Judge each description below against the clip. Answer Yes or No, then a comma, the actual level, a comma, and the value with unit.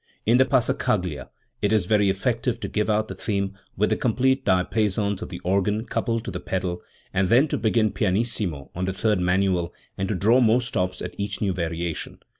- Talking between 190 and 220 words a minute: Yes, average, 200 wpm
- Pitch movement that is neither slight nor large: Yes, average, 3.6 semitones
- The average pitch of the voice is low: Yes, low, 105 Hz